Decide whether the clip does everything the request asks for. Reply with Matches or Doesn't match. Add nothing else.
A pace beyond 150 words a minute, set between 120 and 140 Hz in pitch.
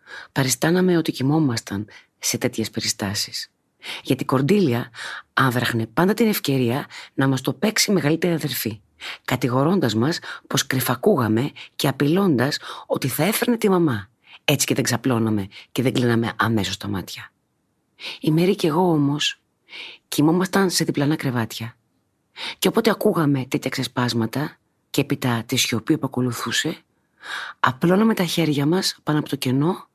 Doesn't match